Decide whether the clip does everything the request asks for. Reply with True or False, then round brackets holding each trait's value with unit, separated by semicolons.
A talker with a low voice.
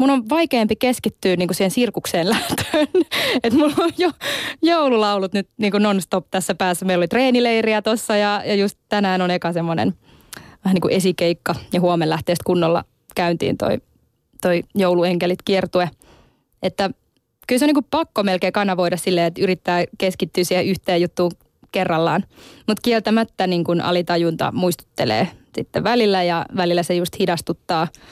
False (190 Hz)